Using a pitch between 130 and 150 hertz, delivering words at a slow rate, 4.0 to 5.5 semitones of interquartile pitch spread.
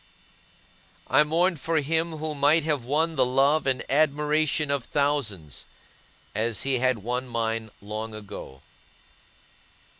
Yes: medium, 140 Hz; slow, 125 wpm; average, 4.7 semitones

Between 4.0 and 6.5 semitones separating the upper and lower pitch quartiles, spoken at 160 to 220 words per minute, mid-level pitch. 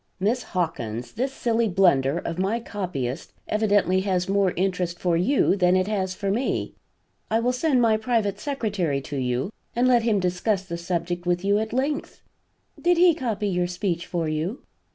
No: average, 4.3 semitones; average, 175 wpm; high, 195 Hz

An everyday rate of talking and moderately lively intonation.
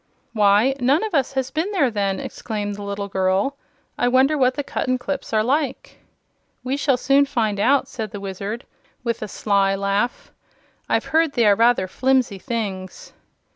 Yes: average, 170 wpm; average, 5.0 semitones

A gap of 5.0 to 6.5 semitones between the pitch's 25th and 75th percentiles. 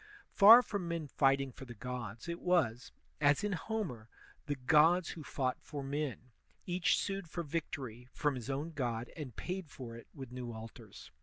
Yes: wide, 5.4 semitones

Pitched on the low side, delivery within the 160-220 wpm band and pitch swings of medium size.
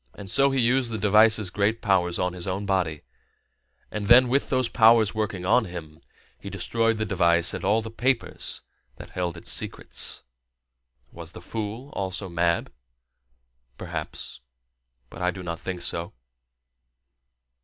No: low, 100 Hz; average, 150 wpm; average, 4.1 semitones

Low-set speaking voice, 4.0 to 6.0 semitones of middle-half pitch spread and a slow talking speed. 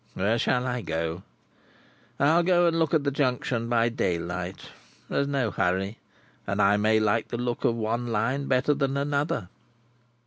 No: low, 120 Hz; average, 5.1 semitones; average, 165 wpm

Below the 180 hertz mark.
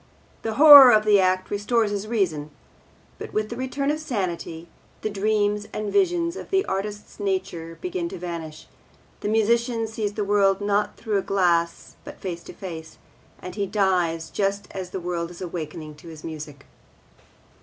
No: high, 200 Hz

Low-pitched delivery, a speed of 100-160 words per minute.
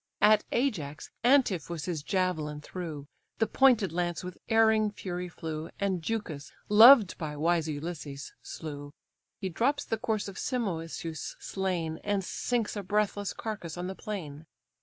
No: medium, 180 Hz; average, 140 wpm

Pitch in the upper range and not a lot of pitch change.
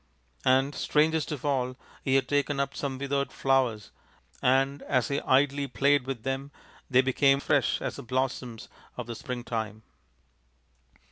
No: low, 135 Hz; narrow, 1.8 semitones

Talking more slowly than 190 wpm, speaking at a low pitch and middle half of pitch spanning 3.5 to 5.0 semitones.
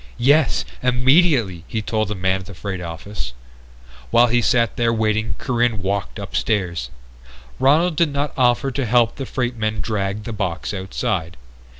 Yes: average, 160 wpm; low, 110 Hz; average, 4.2 semitones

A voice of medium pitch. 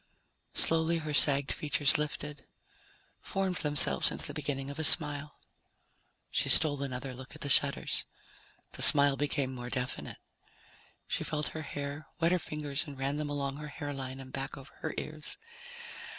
Yes: medium, 145 Hz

